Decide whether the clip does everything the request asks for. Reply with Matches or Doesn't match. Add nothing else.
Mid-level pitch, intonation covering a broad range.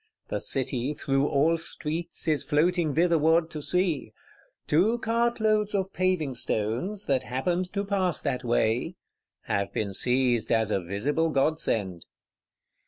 Matches